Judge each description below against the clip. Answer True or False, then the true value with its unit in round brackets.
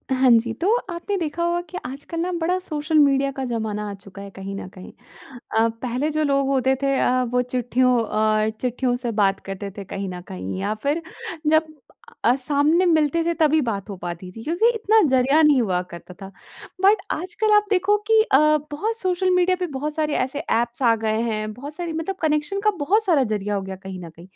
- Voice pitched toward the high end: True (270 Hz)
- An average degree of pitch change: False (7.4 semitones)